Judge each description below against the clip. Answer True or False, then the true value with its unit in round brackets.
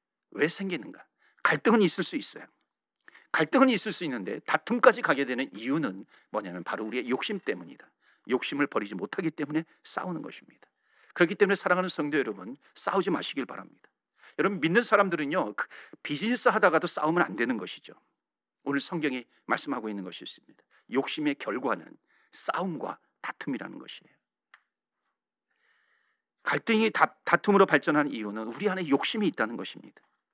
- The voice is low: False (180 Hz)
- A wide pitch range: True (7.8 semitones)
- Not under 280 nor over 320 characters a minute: False (365 characters per minute)